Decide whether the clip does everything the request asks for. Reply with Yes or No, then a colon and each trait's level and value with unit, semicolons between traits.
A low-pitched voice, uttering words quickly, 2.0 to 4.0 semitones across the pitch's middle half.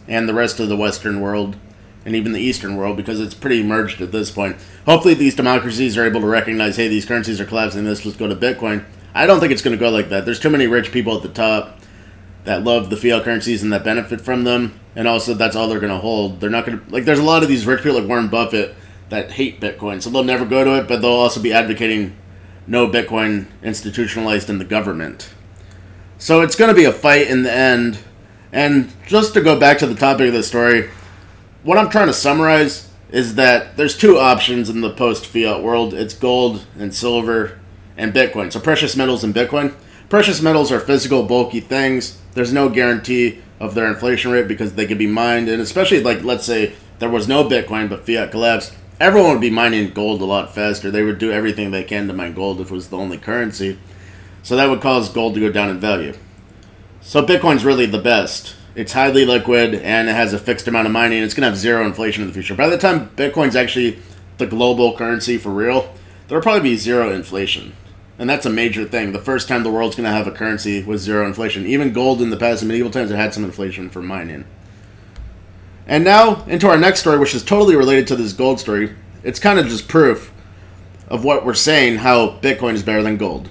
Yes: low, 110 Hz; fast, 225 wpm; average, 3.4 semitones